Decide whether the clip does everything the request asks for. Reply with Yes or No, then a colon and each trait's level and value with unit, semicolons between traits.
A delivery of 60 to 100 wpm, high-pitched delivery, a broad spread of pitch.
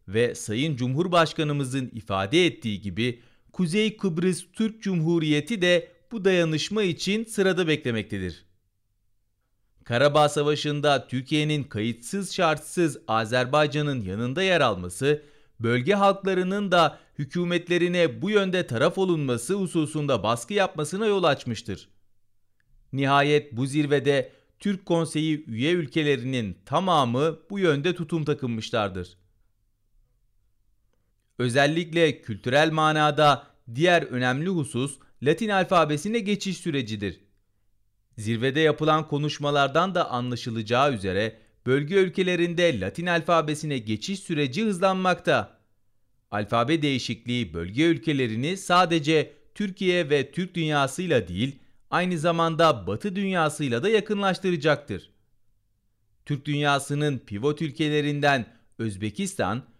No: slow, 95 wpm; medium, 145 Hz; wide, 6.8 semitones